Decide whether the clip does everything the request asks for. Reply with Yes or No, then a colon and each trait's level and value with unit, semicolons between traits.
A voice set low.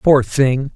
Yes: low, 130 Hz